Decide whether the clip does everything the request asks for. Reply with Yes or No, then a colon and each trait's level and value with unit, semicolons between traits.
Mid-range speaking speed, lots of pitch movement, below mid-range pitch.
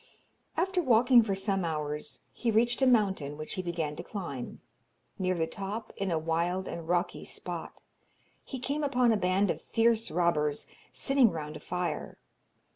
No: average, 165 wpm; wide, 6.0 semitones; high, 190 Hz